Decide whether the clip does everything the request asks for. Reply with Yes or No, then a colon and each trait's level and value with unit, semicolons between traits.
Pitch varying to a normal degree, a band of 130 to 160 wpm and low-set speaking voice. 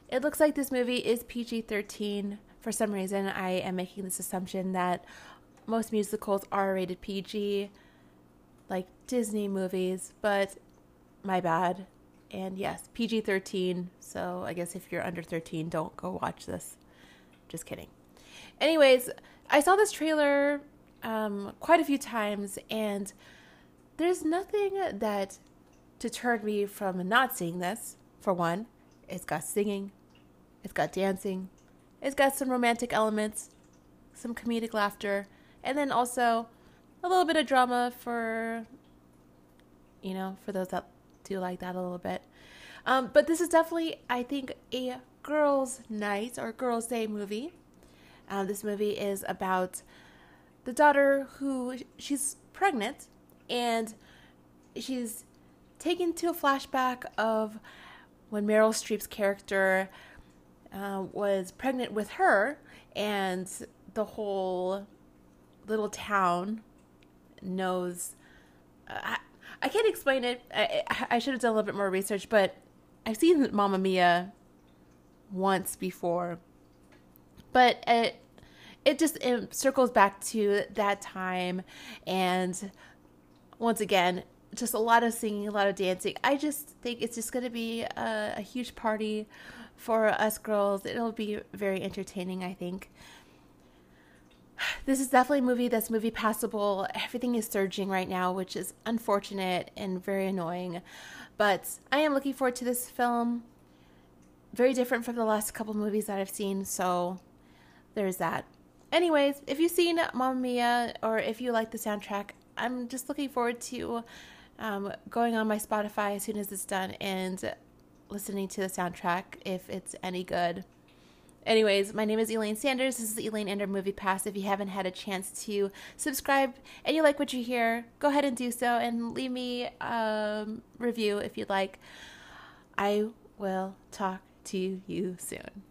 No: average, 4.6 semitones; average, 150 wpm; high, 205 Hz